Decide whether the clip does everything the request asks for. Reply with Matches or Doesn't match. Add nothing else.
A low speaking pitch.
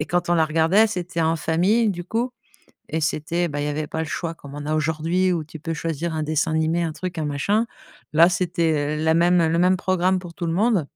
Doesn't match